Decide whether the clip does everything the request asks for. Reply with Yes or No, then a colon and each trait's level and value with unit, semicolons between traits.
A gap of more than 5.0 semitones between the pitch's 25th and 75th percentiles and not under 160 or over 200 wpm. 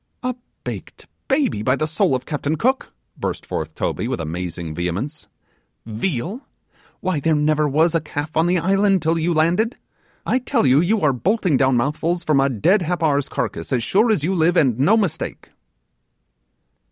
Yes: wide, 5.4 semitones; average, 175 wpm